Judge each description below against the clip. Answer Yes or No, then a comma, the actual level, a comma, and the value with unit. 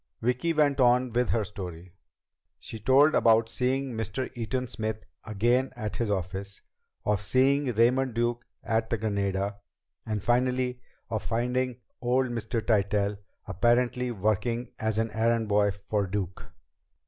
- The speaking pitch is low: Yes, low, 115 Hz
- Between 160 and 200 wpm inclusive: No, slow, 135 wpm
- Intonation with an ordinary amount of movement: Yes, average, 3.2 semitones